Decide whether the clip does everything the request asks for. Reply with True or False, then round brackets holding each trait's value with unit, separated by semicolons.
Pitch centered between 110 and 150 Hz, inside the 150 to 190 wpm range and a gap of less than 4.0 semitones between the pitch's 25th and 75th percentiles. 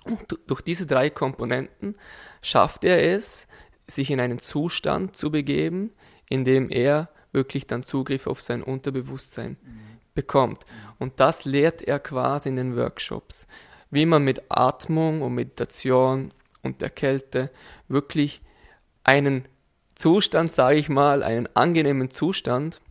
False (135 Hz; 130 wpm; 2.9 semitones)